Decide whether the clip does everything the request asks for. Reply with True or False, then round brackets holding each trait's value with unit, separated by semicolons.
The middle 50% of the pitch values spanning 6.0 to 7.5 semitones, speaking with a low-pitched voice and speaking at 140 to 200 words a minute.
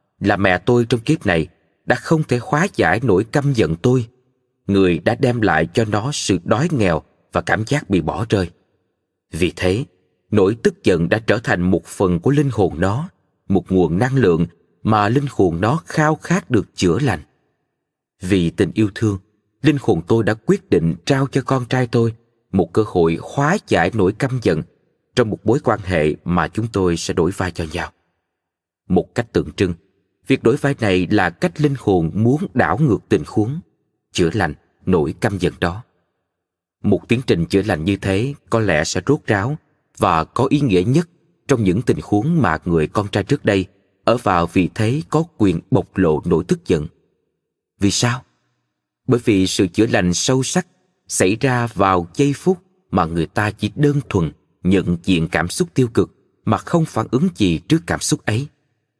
True (7.1 semitones; 105 Hz; 190 wpm)